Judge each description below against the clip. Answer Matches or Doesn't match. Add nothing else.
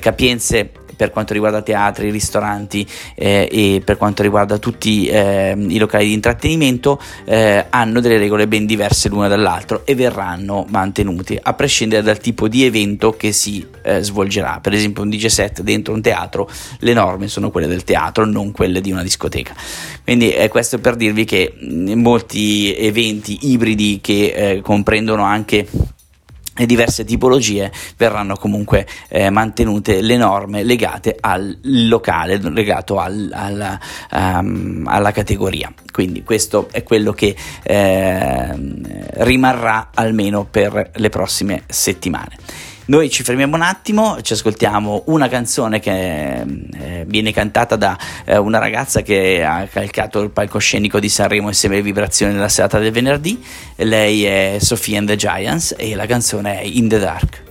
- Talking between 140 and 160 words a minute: Matches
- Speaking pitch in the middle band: Doesn't match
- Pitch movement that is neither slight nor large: Doesn't match